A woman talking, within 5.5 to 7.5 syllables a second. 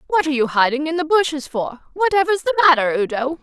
Yes: female; 6.5 syllables/s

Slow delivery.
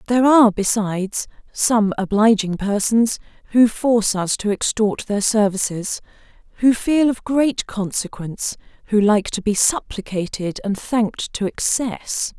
Yes: slow, 130 wpm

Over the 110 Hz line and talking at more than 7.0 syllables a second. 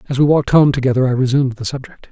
Yes: low, 135 Hz; 7.8 syllables/s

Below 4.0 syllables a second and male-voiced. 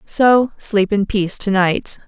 No: 3.7 syllables/s; female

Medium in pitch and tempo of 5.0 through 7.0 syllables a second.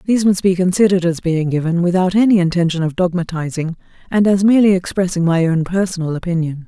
Yes: medium, 180 Hz; 6.5 syllables/s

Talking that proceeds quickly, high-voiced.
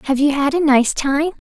Yes: fast, 245 wpm; very high, 285 Hz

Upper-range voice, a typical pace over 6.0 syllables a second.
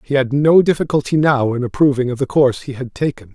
No: low, 135 Hz; 6.2 syllables/s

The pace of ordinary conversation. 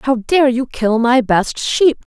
Yes: average, 195 wpm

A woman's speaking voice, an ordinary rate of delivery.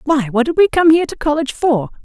No: female; fast, 265 wpm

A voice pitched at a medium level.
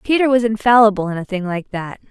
No: high, 215 Hz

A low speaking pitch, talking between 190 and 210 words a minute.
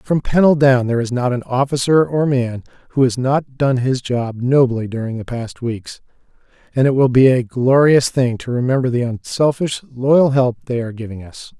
Yes: low, 125 Hz; average, 195 wpm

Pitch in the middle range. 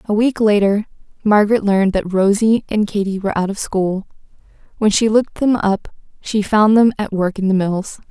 No: high, 205 Hz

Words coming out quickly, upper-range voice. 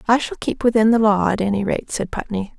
Yes: fast, 255 wpm; high, 210 Hz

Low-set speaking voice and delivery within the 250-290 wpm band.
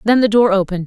No: high, 210 Hz; fast, 280 wpm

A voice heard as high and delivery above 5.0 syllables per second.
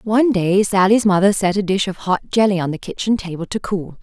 Yes: high, 195 Hz; 5.6 syllables/s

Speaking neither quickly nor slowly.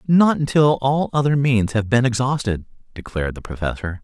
Yes: average, 165 wpm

